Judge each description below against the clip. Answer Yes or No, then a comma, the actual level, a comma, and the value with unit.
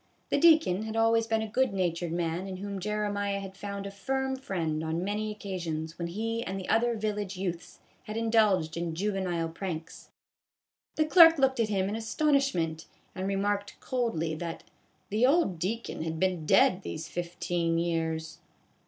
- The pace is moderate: Yes, average, 175 wpm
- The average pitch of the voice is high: Yes, high, 195 Hz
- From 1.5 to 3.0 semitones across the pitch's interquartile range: No, average, 4.6 semitones